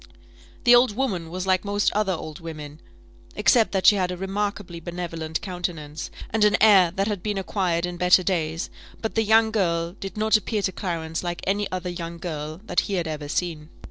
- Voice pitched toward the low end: No, medium, 180 Hz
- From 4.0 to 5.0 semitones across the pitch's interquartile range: No, average, 3.5 semitones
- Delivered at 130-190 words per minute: No, average, 200 wpm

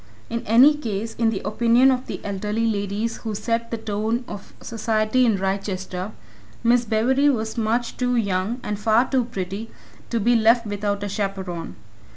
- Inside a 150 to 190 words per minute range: Yes, average, 170 wpm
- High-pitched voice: Yes, high, 220 Hz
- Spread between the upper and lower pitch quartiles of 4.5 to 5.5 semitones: No, average, 2.7 semitones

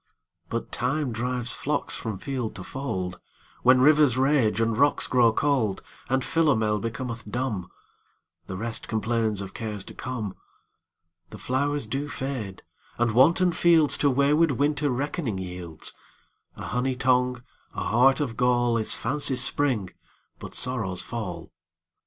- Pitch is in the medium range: No, low, 125 Hz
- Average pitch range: Yes, average, 4.2 semitones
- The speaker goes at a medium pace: No, slow, 120 wpm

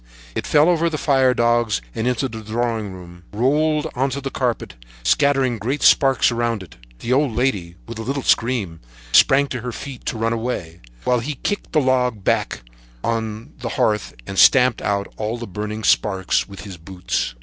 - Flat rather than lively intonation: No, average, 4.0 semitones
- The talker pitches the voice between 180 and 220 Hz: No, low, 120 Hz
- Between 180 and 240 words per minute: Yes, average, 185 wpm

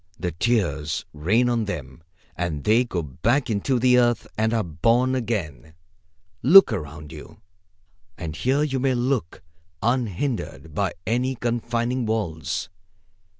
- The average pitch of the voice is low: Yes, low, 110 Hz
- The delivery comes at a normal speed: No, slow, 130 wpm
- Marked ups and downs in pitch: Yes, wide, 7.3 semitones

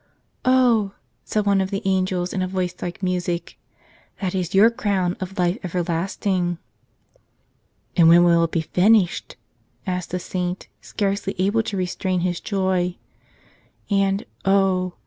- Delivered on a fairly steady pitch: Yes, narrow, 1.8 semitones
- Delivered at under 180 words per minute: Yes, average, 140 wpm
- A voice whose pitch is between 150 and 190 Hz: Yes, medium, 185 Hz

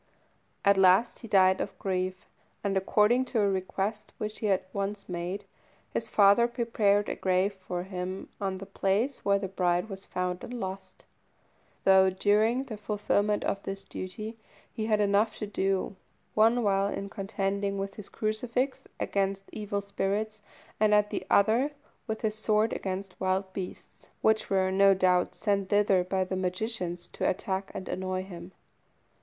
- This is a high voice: Yes, high, 200 Hz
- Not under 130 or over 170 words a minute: Yes, average, 160 wpm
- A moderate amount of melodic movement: No, narrow, 2.1 semitones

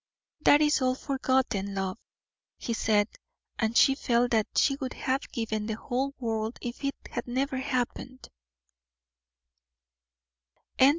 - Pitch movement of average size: Yes, average, 3.2 semitones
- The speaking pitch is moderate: No, high, 245 Hz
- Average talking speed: No, slow, 125 wpm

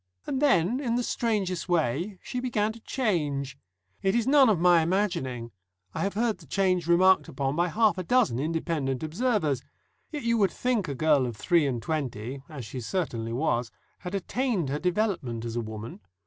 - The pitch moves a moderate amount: No, wide, 7.7 semitones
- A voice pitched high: No, medium, 175 Hz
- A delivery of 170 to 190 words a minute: Yes, average, 185 wpm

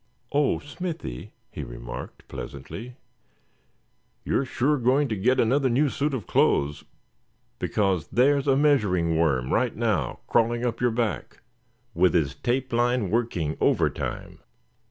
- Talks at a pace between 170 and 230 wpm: No, slow, 135 wpm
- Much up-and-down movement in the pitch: Yes, wide, 6.9 semitones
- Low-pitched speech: Yes, low, 120 Hz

